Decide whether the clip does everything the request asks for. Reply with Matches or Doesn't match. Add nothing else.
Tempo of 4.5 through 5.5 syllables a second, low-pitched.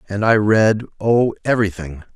Matches